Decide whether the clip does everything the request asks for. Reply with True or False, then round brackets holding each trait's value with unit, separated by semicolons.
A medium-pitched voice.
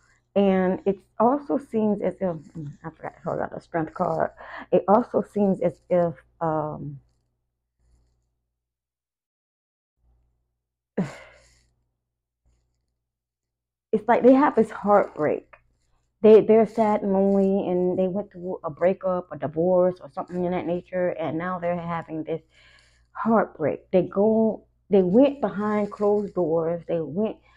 True (175 Hz)